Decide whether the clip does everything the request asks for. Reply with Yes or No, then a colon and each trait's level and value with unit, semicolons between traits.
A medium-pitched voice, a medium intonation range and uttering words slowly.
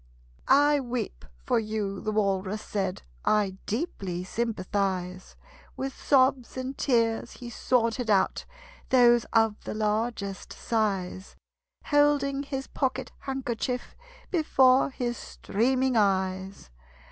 No: high, 225 Hz; average, 4.7 semitones; slow, 105 wpm